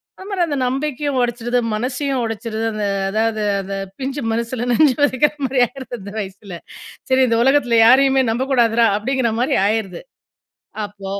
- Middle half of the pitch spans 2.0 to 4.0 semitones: Yes, average, 3.3 semitones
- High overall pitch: Yes, high, 245 Hz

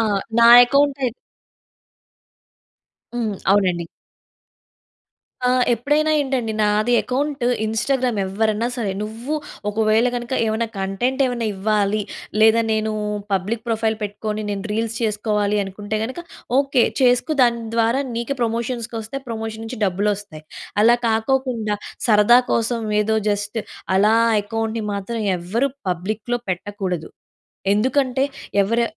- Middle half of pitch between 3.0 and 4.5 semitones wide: No, narrow, 2.6 semitones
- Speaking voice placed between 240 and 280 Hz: No, high, 225 Hz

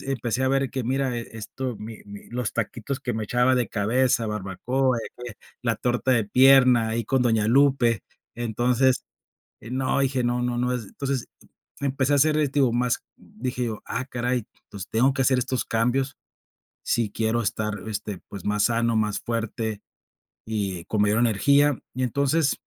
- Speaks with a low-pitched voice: Yes, low, 120 Hz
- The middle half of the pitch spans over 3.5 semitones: No, average, 2.9 semitones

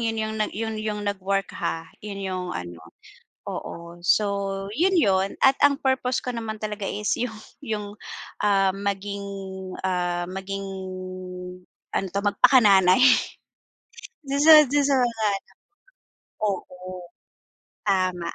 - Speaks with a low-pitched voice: No, high, 200 Hz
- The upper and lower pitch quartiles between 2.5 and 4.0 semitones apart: Yes, average, 2.8 semitones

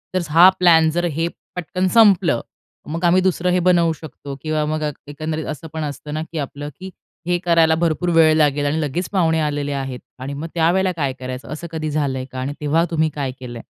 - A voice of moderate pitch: Yes, medium, 155 Hz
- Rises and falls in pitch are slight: No, average, 3.0 semitones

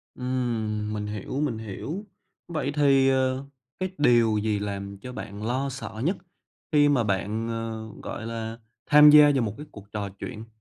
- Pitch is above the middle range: No, low, 115 Hz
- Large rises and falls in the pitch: No, average, 4.3 semitones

